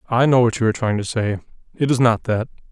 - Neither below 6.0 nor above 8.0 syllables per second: Yes, 6.7 syllables/s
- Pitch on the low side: Yes, low, 115 Hz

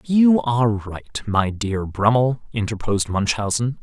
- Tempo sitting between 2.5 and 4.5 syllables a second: Yes, 4.2 syllables/s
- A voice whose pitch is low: Yes, low, 115 Hz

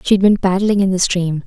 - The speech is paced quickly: Yes, fast, 245 wpm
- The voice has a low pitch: No, high, 190 Hz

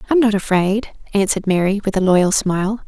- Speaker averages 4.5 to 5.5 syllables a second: No, 5.8 syllables/s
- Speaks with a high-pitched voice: Yes, high, 200 Hz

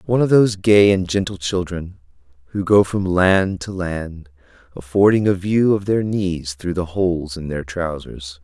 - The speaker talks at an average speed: Yes, average, 180 wpm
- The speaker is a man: Yes, male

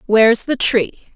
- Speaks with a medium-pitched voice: No, high, 215 Hz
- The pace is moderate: Yes, average, 155 wpm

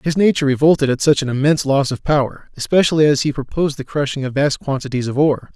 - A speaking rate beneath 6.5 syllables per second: No, 6.9 syllables/s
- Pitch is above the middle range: No, medium, 140 Hz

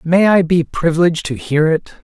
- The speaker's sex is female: No, male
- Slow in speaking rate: No, average, 200 wpm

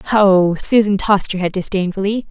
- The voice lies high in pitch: Yes, high, 195 Hz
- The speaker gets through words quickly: No, average, 155 wpm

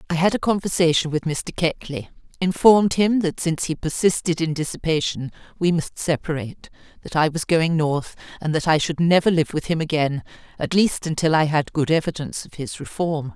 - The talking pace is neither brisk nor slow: Yes, average, 190 wpm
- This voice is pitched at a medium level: Yes, medium, 160 Hz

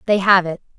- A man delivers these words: No, female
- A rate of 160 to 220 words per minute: No, fast, 230 wpm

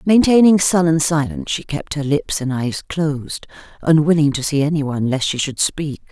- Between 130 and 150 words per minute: No, average, 175 wpm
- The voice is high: No, medium, 155 Hz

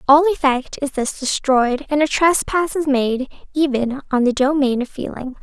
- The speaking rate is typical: Yes, average, 175 wpm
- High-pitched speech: Yes, very high, 275 Hz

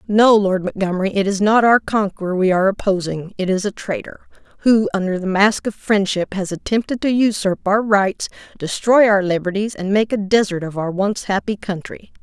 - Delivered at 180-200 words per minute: Yes, average, 190 wpm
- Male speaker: No, female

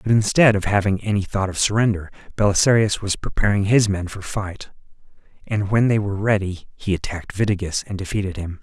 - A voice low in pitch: Yes, low, 100 Hz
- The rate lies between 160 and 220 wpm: Yes, average, 180 wpm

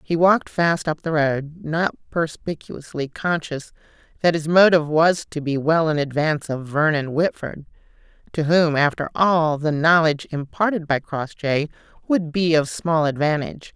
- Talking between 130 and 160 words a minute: Yes, average, 155 wpm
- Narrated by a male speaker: No, female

